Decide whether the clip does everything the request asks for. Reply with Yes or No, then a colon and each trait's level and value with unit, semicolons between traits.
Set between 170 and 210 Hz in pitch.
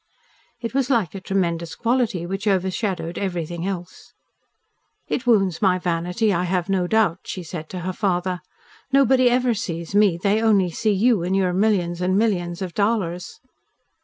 Yes: high, 190 Hz